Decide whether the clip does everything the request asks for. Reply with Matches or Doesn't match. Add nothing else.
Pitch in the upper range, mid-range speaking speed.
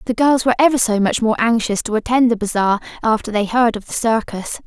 Doesn't match